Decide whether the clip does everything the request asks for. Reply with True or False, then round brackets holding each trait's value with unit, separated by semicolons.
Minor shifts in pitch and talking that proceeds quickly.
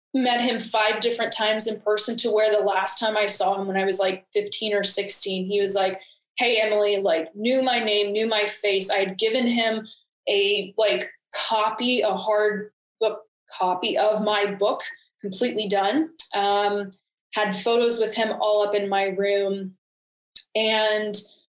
False (1.8 semitones; 170 wpm)